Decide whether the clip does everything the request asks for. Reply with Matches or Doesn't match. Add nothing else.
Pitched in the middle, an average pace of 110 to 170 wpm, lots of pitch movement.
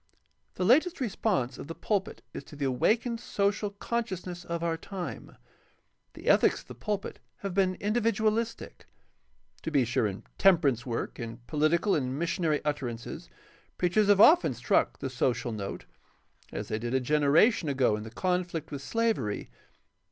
Matches